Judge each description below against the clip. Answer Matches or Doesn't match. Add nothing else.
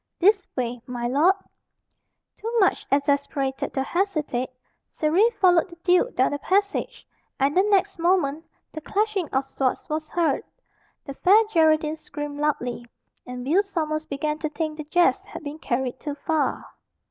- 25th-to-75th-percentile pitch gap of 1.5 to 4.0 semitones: Doesn't match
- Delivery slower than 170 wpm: Matches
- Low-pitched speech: Doesn't match